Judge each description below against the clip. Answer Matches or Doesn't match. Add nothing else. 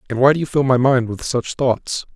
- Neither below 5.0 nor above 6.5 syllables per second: Matches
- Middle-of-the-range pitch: Doesn't match